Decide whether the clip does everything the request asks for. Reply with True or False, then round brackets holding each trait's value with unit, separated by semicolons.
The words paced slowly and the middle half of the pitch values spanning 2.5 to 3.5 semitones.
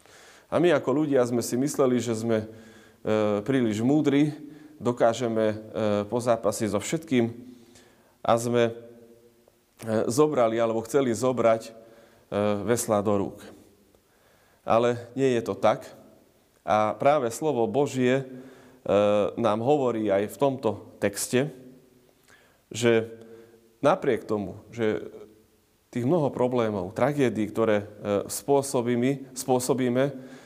True (100 wpm; 2.8 semitones)